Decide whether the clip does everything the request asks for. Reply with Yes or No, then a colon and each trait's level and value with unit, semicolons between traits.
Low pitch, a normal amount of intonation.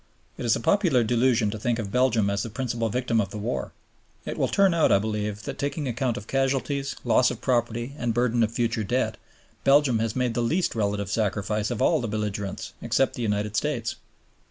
Yes: low, 115 Hz; average, 3.2 semitones